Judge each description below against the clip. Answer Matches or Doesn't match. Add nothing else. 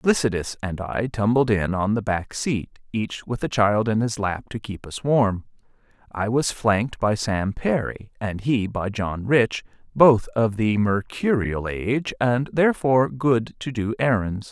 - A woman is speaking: Doesn't match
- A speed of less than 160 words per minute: Doesn't match